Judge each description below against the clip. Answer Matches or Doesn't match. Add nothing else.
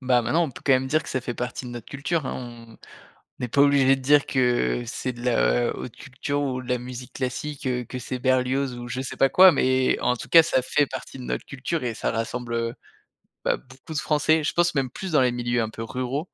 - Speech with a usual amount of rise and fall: Doesn't match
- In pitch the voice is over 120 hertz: Matches